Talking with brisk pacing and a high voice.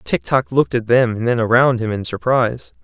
No: fast, 235 wpm; low, 115 Hz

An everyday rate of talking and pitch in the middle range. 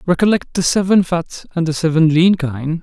Yes: average, 190 wpm; medium, 170 Hz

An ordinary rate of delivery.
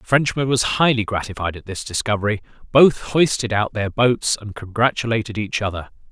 Yes: average, 165 wpm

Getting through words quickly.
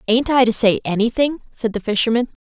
No: average, 195 wpm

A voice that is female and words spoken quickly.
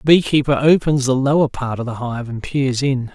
No: male; fast, 230 wpm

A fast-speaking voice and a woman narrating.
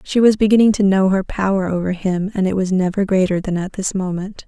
Yes: fast, 240 wpm; female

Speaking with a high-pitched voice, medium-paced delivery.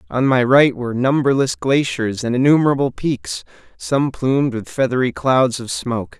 No: low, 130 Hz; average, 155 wpm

